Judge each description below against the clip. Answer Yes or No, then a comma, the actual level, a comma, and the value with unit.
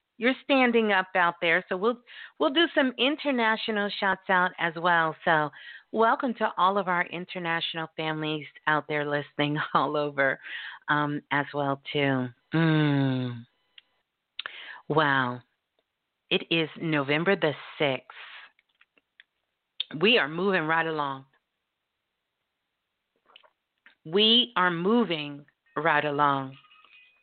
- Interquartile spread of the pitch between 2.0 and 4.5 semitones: No, average, 5.3 semitones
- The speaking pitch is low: No, medium, 165 Hz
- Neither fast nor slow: No, slow, 110 wpm